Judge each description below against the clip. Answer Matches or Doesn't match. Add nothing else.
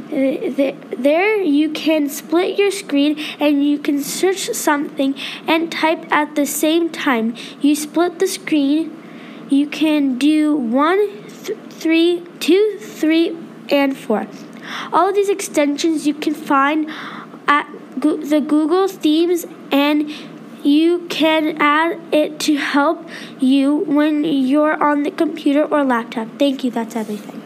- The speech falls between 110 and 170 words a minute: Matches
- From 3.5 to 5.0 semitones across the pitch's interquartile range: Doesn't match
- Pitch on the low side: Doesn't match